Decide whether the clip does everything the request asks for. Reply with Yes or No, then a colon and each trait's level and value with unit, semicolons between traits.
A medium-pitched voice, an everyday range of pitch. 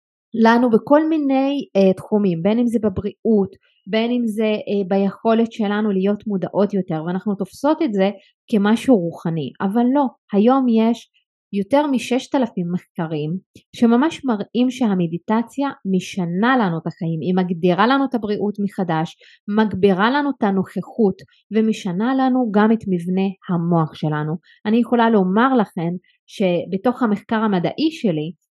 No: high, 210 Hz; average, 4.1 semitones